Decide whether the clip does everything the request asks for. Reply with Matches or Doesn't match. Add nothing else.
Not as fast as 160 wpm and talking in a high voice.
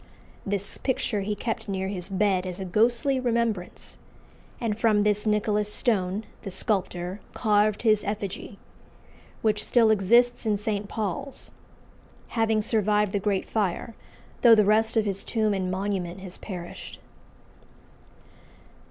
Matches